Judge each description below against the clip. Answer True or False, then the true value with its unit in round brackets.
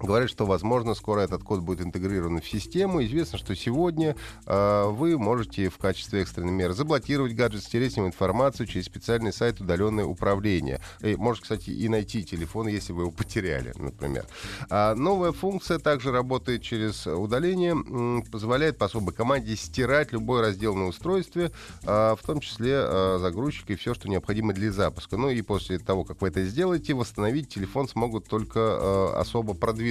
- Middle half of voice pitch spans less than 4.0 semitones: False (4.5 semitones)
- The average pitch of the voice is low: True (110 Hz)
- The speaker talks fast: True (170 wpm)